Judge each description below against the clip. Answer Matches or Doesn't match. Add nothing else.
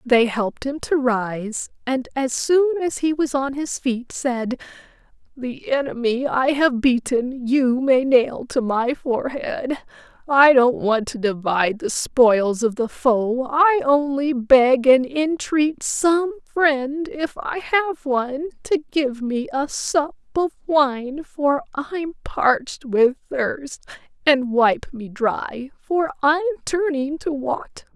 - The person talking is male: Doesn't match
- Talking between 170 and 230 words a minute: Doesn't match